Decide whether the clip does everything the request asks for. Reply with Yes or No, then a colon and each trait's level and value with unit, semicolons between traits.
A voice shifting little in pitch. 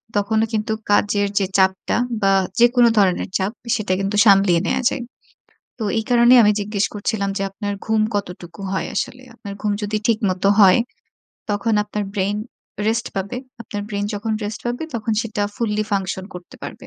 Yes: narrow, 1.9 semitones